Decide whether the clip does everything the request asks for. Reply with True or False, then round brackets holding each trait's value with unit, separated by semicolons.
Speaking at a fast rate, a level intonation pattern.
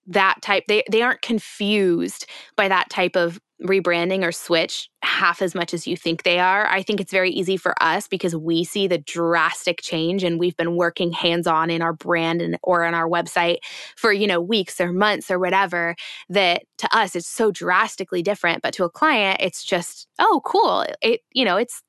True (210 wpm; 2.2 semitones)